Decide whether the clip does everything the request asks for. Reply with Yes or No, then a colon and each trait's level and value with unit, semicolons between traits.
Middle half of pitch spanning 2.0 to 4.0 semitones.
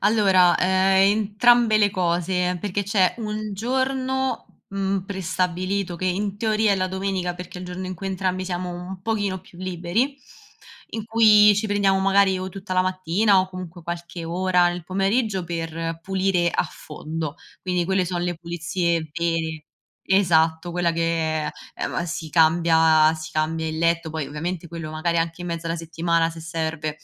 Yes: narrow, 2.6 semitones